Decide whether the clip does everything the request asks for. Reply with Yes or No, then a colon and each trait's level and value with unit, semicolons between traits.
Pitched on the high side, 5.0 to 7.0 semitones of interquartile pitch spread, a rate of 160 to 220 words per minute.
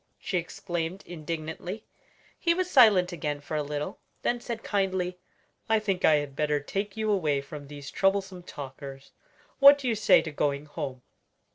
No: medium, 175 Hz; wide, 5.5 semitones; average, 165 wpm